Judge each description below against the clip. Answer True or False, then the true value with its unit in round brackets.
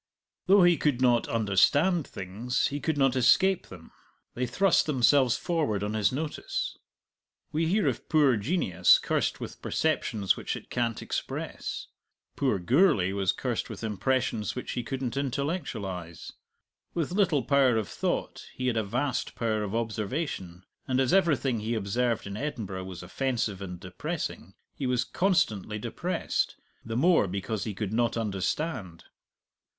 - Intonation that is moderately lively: False (5.9 semitones)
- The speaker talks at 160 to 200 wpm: False (150 wpm)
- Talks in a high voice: False (120 Hz)